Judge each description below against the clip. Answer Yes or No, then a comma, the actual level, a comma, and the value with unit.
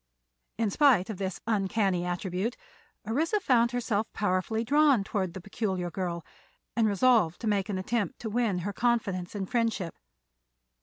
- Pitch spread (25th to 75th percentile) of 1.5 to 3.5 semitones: No, average, 3.9 semitones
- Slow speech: No, average, 150 wpm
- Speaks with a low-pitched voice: No, high, 205 Hz